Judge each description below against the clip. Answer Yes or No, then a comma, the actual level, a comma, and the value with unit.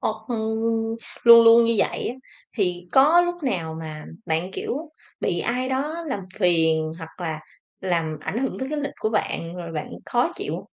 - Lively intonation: Yes, wide, 7.9 semitones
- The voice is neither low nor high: No, high, 195 Hz